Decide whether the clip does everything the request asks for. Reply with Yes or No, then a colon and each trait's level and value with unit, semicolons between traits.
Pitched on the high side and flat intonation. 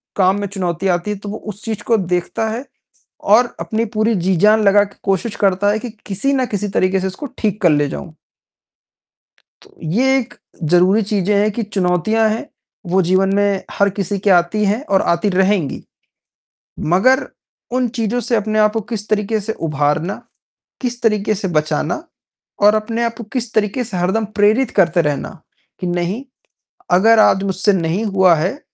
No: high, 205 Hz; average, 3.1 semitones